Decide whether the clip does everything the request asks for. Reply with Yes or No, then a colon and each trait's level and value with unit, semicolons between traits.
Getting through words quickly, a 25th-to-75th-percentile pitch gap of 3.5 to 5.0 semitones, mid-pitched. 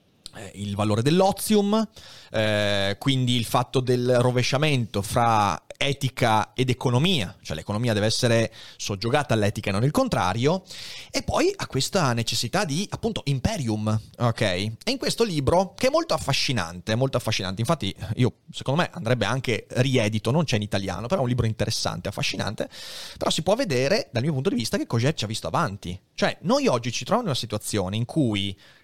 No: fast, 175 wpm; average, 4.5 semitones; low, 120 Hz